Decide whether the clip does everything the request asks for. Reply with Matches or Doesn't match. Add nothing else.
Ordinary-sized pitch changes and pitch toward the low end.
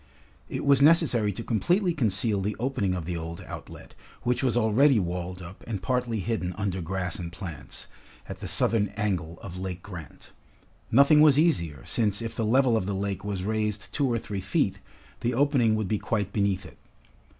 Matches